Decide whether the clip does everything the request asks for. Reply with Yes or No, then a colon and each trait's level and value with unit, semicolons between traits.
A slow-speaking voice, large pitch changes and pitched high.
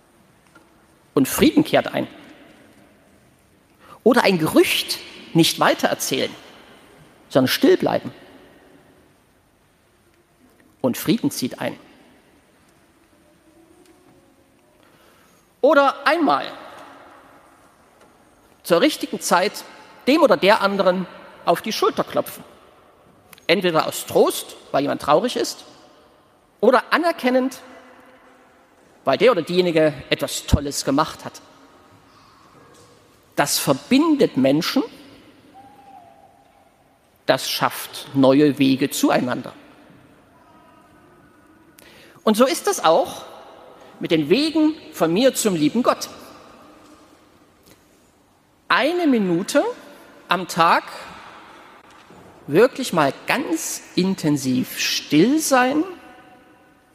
Yes: slow, 80 wpm; wide, 8.7 semitones; very high, 270 Hz